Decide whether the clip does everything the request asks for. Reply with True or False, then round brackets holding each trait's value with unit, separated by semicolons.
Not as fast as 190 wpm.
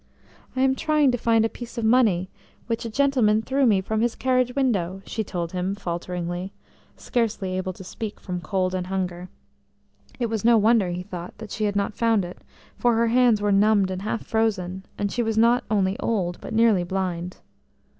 False (195 wpm)